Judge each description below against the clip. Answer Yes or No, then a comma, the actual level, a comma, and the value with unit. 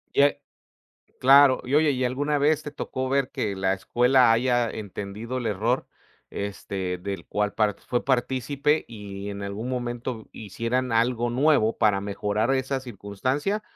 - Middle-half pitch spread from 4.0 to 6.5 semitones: Yes, average, 4.4 semitones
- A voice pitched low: Yes, low, 120 Hz